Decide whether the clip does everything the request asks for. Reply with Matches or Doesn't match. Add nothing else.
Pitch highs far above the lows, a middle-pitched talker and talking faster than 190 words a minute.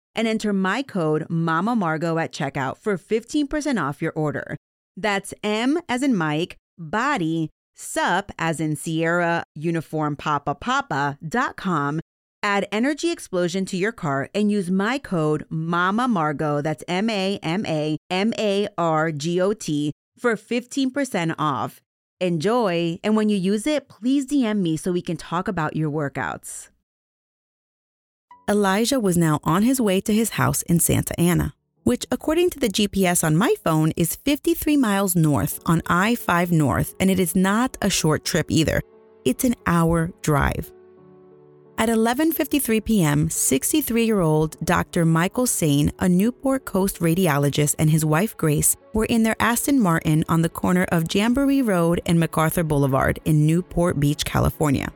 Doesn't match